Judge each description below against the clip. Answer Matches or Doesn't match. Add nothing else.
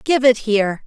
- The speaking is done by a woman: Matches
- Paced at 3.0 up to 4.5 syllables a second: Doesn't match